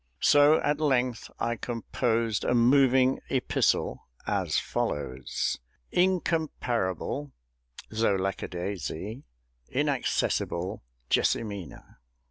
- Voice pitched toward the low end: Yes, low, 120 Hz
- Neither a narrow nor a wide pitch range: No, wide, 5.8 semitones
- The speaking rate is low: Yes, slow, 85 wpm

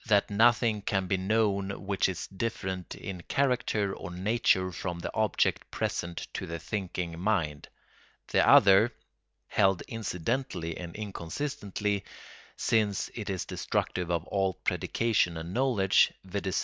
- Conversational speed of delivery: No, slow, 130 wpm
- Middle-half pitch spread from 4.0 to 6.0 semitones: No, average, 3.2 semitones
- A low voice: Yes, very low, 95 Hz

